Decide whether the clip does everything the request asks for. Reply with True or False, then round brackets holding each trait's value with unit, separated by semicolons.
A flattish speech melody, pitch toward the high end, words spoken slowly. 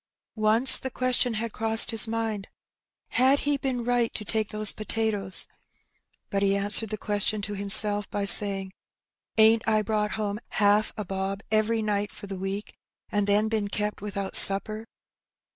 False (1.7 semitones; 210 Hz; 165 wpm)